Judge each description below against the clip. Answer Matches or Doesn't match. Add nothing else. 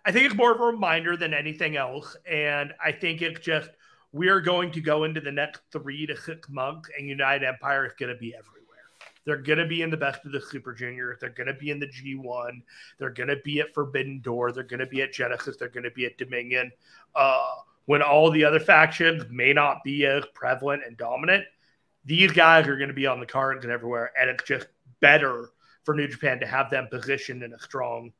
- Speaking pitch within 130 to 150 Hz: Matches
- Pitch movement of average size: Matches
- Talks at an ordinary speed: Doesn't match